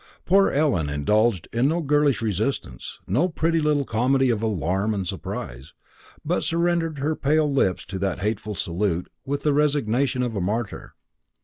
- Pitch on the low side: Yes, low, 120 Hz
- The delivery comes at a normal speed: Yes, average, 155 wpm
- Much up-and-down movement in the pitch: Yes, wide, 7.0 semitones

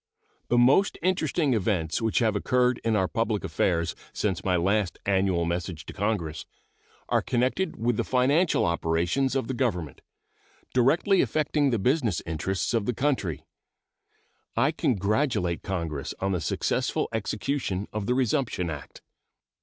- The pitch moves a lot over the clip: Yes, wide, 6.1 semitones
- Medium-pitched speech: No, low, 110 Hz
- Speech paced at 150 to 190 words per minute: No, average, 140 wpm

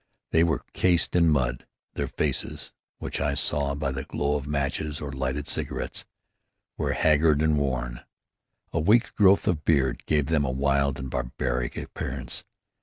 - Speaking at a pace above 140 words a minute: Yes, average, 160 wpm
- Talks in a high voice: No, very low, 70 Hz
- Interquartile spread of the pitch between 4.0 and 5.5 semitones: No, narrow, 2.6 semitones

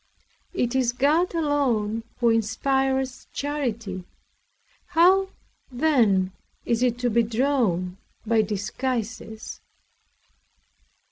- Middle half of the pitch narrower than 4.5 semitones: Yes, average, 4.1 semitones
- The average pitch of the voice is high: Yes, high, 245 Hz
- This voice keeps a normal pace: No, slow, 85 wpm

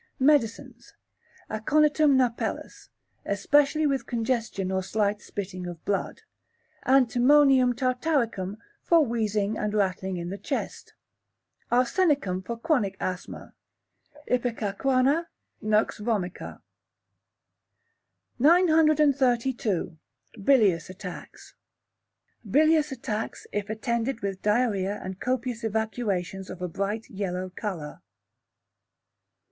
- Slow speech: Yes, slow, 90 wpm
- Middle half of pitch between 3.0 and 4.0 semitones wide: No, average, 5.1 semitones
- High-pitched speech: Yes, high, 225 Hz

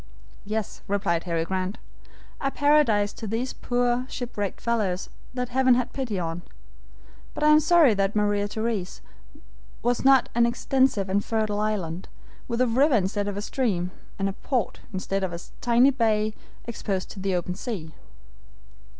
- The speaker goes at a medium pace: Yes, average, 160 wpm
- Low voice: No, high, 215 Hz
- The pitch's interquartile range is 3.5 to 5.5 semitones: Yes, average, 4.1 semitones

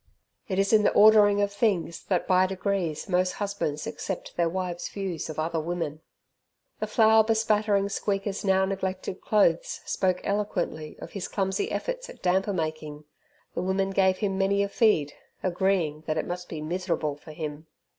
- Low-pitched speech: No, high, 190 Hz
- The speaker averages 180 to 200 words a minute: No, average, 165 wpm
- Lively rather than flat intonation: No, average, 3.2 semitones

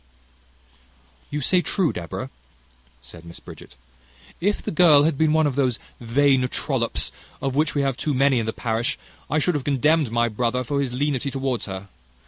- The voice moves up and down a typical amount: Yes, average, 3.8 semitones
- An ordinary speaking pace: Yes, average, 180 wpm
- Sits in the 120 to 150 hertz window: Yes, low, 135 Hz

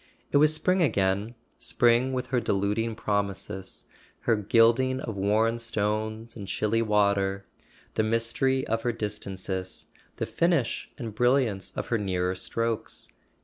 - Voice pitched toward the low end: Yes, low, 110 Hz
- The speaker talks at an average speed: No, slow, 130 wpm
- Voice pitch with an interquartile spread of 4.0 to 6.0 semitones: No, average, 2.9 semitones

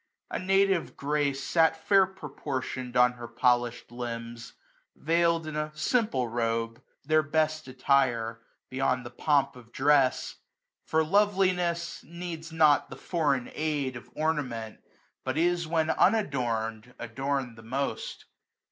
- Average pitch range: Yes, average, 4.8 semitones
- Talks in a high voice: No, medium, 140 Hz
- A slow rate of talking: Yes, slow, 130 wpm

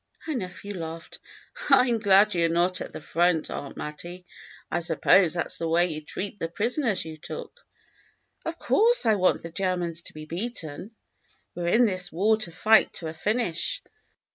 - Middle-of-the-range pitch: Yes, medium, 180 Hz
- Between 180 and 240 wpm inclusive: Yes, average, 195 wpm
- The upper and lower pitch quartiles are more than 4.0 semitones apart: Yes, average, 4.7 semitones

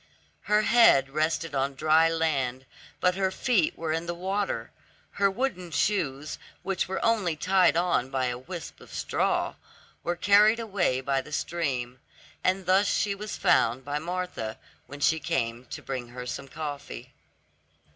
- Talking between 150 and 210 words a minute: Yes, average, 155 wpm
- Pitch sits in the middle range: Yes, medium, 165 Hz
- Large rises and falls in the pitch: Yes, wide, 5.8 semitones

